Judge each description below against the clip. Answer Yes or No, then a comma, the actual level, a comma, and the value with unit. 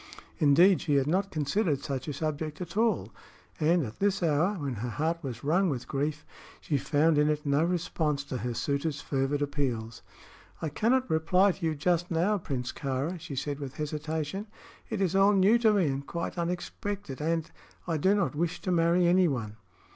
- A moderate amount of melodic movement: Yes, average, 4.2 semitones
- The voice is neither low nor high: Yes, medium, 155 Hz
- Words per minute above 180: Yes, average, 190 wpm